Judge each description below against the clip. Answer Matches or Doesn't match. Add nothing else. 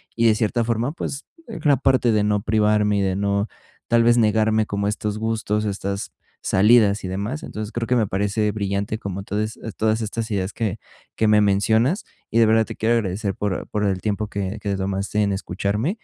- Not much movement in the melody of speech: Matches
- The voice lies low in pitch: Matches